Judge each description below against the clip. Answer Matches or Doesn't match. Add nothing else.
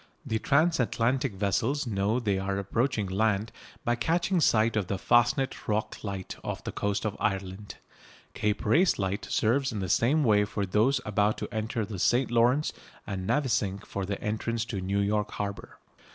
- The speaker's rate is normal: Matches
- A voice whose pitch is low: Matches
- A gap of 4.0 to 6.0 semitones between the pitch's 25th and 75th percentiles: Doesn't match